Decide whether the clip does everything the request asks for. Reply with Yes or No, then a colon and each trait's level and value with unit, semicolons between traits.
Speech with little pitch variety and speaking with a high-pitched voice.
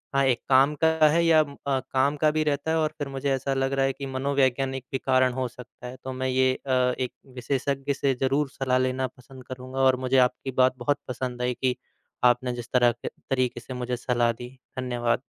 No: narrow, 1.5 semitones; low, 130 Hz